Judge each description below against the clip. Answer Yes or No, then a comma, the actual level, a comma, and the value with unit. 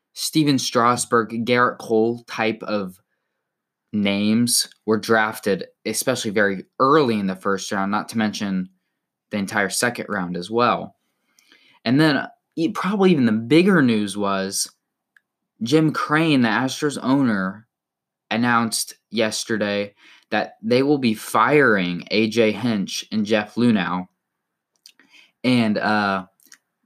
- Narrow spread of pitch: No, average, 3.3 semitones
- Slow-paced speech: Yes, slow, 115 wpm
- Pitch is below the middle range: Yes, low, 110 Hz